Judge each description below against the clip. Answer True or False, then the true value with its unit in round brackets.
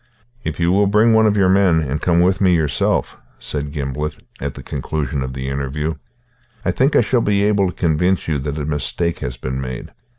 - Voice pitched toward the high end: False (80 Hz)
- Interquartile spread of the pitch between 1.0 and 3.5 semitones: False (5.2 semitones)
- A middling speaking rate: False (210 wpm)